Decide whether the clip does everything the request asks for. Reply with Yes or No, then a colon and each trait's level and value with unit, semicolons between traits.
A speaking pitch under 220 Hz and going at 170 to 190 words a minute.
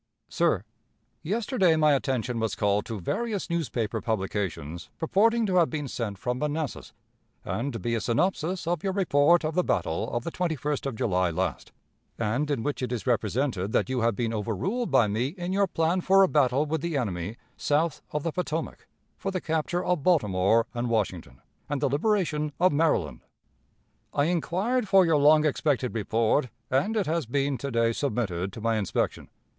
Yes: medium, 140 Hz; average, 180 wpm